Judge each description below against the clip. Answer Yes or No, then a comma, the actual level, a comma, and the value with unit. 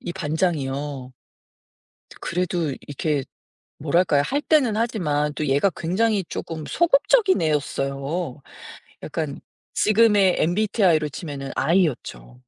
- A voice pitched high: No, medium, 160 Hz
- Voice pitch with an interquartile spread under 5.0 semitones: No, average, 5.3 semitones